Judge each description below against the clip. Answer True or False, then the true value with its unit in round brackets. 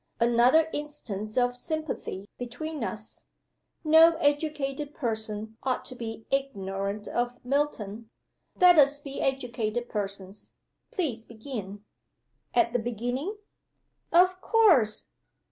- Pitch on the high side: True (245 Hz)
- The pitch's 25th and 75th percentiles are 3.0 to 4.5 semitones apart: False (5.1 semitones)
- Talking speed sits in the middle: False (105 wpm)